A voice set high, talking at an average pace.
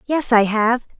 Yes: high, 235 Hz; average, 180 wpm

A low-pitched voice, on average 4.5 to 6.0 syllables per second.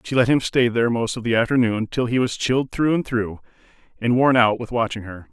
Yes: low, 120 Hz; 5.9 syllables/s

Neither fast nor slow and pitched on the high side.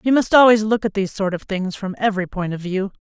No: fast, 280 wpm; high, 200 Hz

